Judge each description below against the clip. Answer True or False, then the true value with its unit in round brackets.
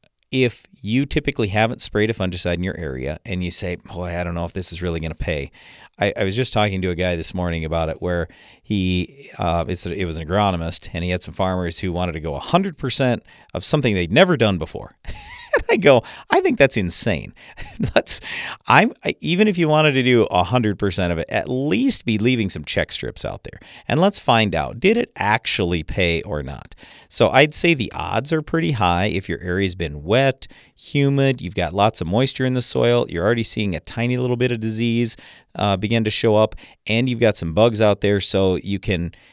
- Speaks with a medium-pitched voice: False (100 Hz)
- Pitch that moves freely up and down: True (5.8 semitones)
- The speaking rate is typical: False (225 wpm)